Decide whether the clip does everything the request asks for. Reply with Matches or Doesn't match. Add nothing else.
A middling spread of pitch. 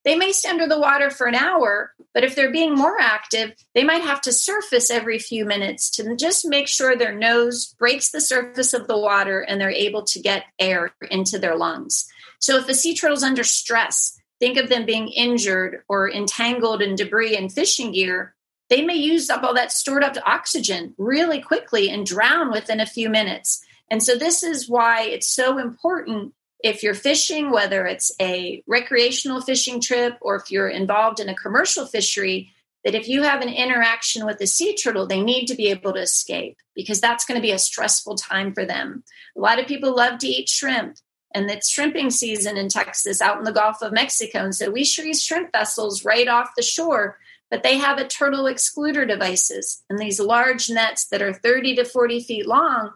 Matches